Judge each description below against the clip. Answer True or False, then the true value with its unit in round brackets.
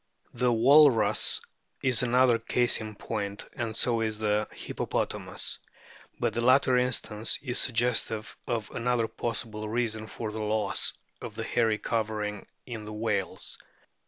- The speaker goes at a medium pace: False (130 wpm)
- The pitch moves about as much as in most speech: False (2.2 semitones)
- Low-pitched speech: True (115 Hz)